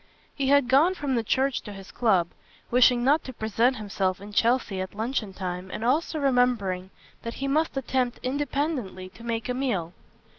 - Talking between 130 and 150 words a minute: No, average, 180 wpm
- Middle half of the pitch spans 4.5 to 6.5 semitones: Yes, average, 5.2 semitones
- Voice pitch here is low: No, high, 240 Hz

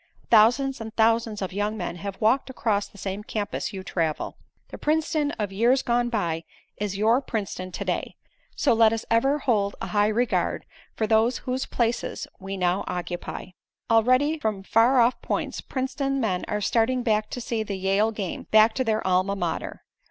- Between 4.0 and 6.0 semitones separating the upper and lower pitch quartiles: No, average, 3.5 semitones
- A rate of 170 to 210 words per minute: Yes, average, 180 wpm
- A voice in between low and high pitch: No, high, 220 Hz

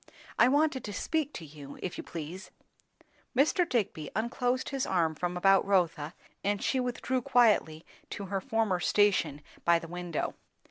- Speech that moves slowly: No, average, 155 wpm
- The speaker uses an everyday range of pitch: No, wide, 6.7 semitones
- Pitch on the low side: No, high, 195 Hz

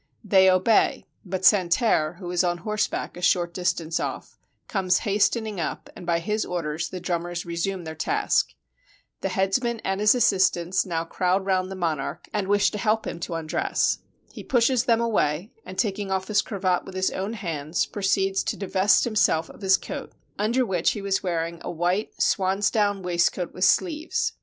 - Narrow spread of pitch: No, average, 3.2 semitones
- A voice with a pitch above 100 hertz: Yes, high, 190 Hz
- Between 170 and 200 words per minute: Yes, average, 185 wpm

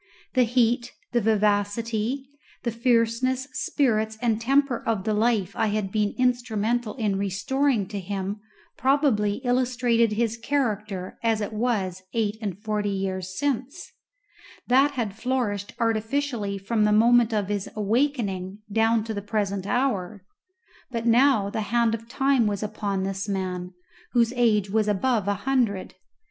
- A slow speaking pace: No, average, 145 wpm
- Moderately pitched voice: No, high, 220 Hz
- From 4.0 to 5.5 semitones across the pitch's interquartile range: No, average, 3.1 semitones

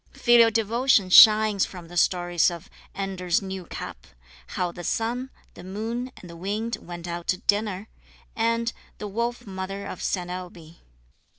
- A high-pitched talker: Yes, high, 195 Hz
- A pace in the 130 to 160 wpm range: Yes, average, 155 wpm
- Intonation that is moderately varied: Yes, average, 4.1 semitones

